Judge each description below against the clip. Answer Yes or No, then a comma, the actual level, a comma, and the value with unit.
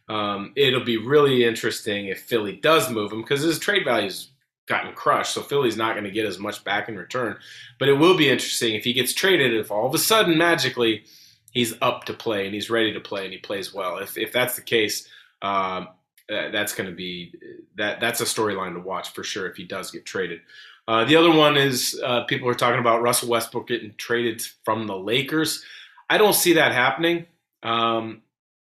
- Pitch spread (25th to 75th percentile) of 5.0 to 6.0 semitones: Yes, wide, 5.6 semitones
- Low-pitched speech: Yes, low, 120 Hz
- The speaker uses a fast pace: Yes, fast, 210 wpm